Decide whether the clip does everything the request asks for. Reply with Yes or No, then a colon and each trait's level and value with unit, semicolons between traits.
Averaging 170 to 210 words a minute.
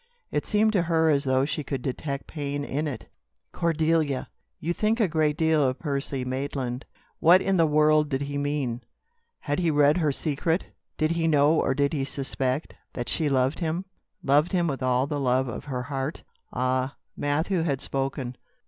Yes: average, 185 wpm